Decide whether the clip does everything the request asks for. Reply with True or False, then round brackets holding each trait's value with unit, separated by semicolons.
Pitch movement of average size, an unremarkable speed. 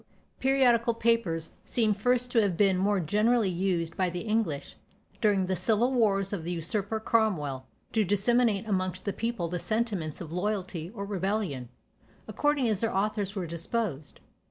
True (4.1 semitones; 160 wpm)